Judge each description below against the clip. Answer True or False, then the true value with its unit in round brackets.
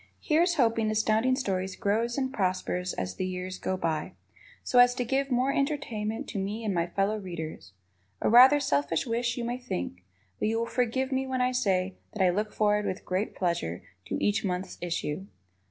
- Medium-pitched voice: False (215 Hz)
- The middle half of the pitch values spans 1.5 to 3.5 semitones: False (5.1 semitones)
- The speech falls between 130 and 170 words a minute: False (190 wpm)